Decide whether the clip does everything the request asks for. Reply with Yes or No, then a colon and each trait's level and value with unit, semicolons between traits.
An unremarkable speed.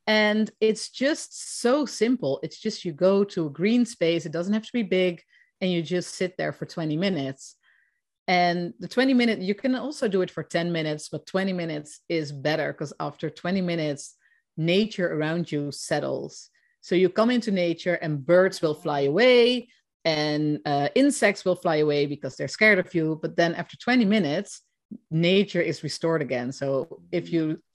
Yes: average, 185 wpm